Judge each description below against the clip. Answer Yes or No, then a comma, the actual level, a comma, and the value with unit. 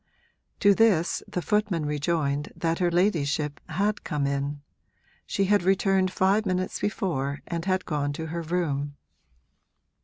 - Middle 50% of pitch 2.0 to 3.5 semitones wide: No, average, 4.5 semitones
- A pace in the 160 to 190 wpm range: No, average, 140 wpm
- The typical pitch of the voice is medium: Yes, medium, 170 Hz